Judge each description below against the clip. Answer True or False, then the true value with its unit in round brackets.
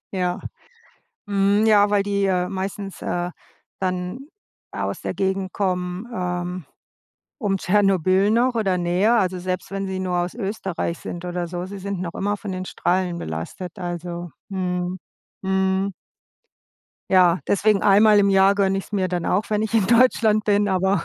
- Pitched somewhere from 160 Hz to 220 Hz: True (190 Hz)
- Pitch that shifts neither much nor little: False (2.0 semitones)